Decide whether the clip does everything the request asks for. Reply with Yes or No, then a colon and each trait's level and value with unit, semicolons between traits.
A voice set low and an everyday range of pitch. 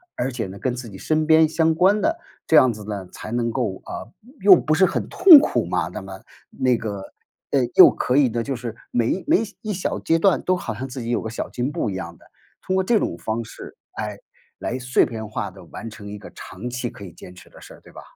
No: low, 120 Hz; wide, 6.7 semitones